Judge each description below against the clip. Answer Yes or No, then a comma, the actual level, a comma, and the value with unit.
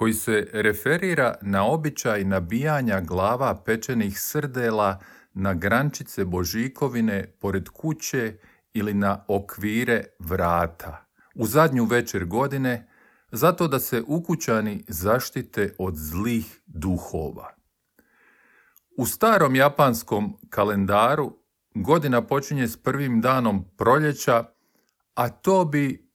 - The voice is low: Yes, low, 115 Hz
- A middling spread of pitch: No, wide, 5.7 semitones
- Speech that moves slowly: Yes, slow, 100 wpm